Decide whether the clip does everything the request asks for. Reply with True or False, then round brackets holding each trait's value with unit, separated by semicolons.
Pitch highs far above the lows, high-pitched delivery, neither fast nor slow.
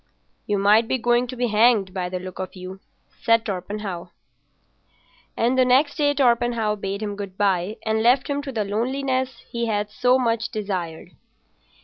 False (3.8 semitones; 220 Hz; 170 wpm)